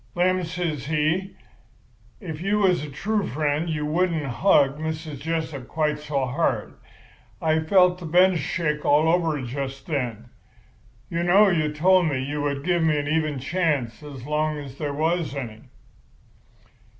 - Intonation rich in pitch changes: No, average, 3.3 semitones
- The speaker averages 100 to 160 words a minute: Yes, average, 155 wpm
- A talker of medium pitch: Yes, medium, 155 Hz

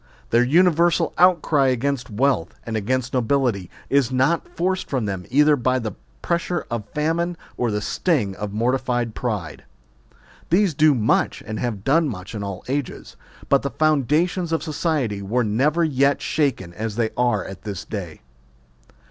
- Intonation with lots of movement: Yes, wide, 6.0 semitones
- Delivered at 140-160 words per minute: Yes, average, 155 wpm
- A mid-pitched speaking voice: No, low, 130 Hz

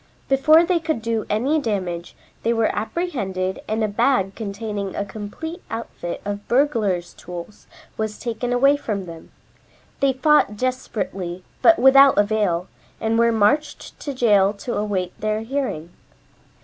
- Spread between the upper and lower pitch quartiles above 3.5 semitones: Yes, average, 4.9 semitones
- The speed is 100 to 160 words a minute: Yes, average, 140 wpm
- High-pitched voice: Yes, high, 220 Hz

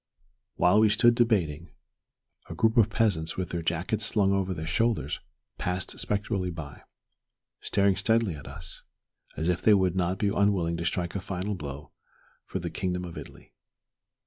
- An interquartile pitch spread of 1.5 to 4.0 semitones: Yes, average, 3.6 semitones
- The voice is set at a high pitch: No, very low, 95 Hz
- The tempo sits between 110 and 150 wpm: No, average, 165 wpm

